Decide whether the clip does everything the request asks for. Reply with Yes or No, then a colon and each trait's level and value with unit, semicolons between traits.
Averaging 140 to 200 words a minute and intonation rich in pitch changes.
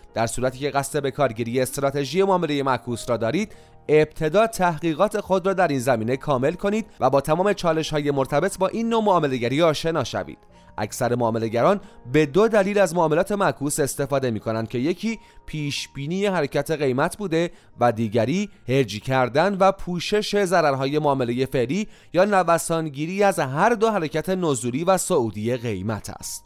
Yes: fast, 155 wpm; wide, 6.6 semitones